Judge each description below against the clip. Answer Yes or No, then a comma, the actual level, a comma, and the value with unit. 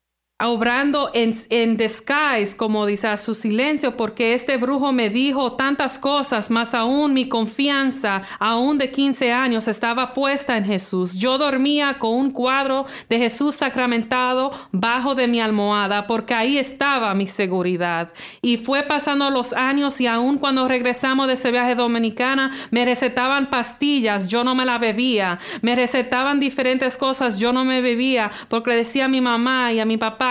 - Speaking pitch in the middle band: No, very high, 250 Hz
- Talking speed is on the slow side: No, average, 165 wpm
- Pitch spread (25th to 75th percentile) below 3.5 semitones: Yes, average, 2.9 semitones